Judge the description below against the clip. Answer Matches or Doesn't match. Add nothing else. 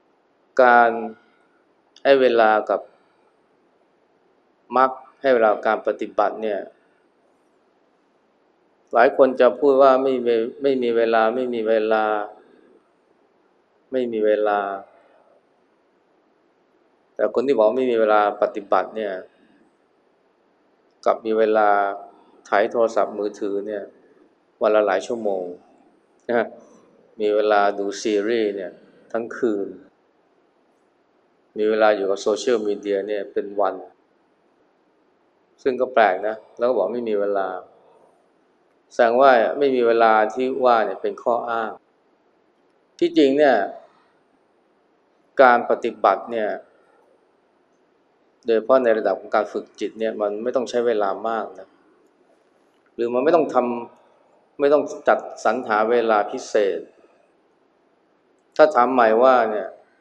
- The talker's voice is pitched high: Doesn't match